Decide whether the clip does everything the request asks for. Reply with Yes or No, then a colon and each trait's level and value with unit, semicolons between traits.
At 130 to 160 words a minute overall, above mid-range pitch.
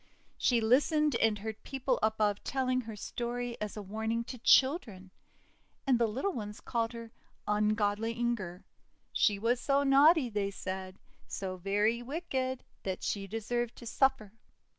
Yes: average, 150 wpm; high, 230 Hz